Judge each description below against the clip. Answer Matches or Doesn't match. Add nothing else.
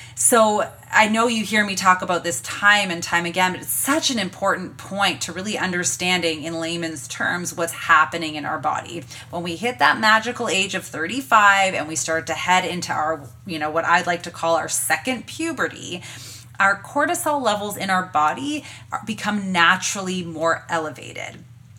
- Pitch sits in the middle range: Matches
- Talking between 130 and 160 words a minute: Doesn't match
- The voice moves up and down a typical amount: Matches